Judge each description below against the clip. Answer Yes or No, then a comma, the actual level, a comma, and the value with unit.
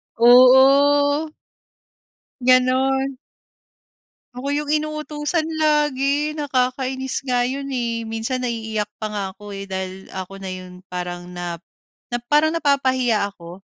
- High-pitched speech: Yes, very high, 255 Hz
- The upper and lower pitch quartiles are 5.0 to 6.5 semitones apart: Yes, average, 5.3 semitones